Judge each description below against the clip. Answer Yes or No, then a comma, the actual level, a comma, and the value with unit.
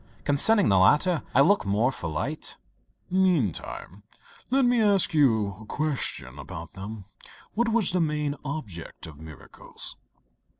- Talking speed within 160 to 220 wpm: No, slow, 135 wpm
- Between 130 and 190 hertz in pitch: Yes, medium, 140 Hz